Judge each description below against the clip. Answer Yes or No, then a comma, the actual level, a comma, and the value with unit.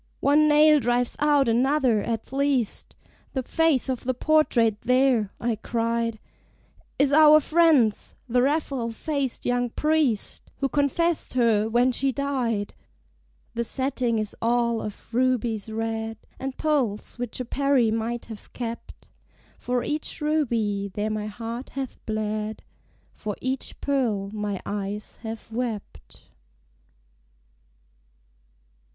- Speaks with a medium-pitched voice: No, high, 240 Hz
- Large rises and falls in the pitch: No, average, 3.7 semitones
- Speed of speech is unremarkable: No, slow, 120 wpm